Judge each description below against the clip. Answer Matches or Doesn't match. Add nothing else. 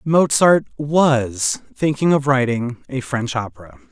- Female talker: Doesn't match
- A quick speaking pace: Doesn't match